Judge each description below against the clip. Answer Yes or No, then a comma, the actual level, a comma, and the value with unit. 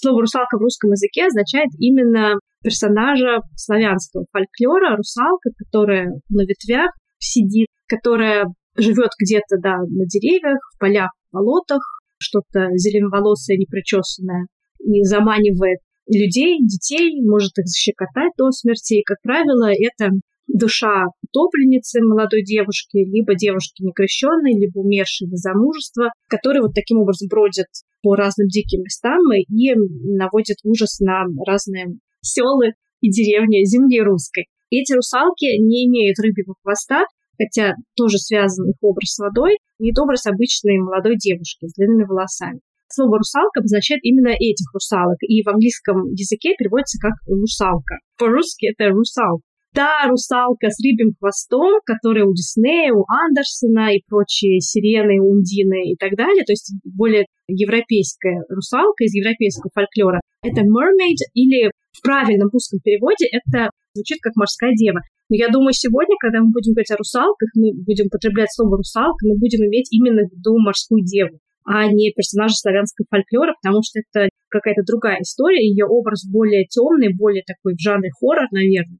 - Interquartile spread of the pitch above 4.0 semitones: No, average, 3.4 semitones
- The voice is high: Yes, high, 215 Hz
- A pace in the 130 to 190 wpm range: Yes, average, 145 wpm